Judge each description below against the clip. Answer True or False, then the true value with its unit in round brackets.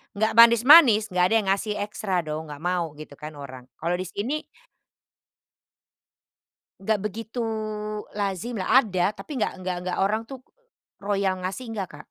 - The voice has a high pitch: True (195 Hz)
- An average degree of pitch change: True (3.8 semitones)